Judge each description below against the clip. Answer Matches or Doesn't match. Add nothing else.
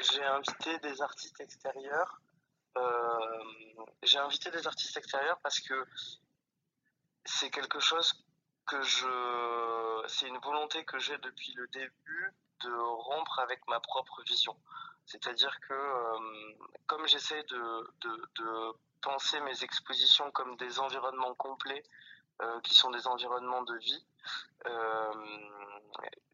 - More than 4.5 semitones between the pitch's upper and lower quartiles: Doesn't match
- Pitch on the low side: Matches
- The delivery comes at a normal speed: Doesn't match